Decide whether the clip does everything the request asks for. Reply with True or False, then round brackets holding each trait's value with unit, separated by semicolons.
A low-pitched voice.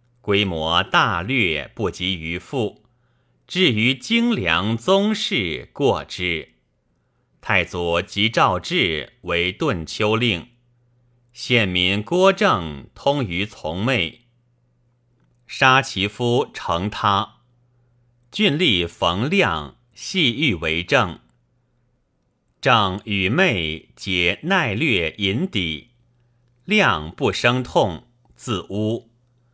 True (110 Hz)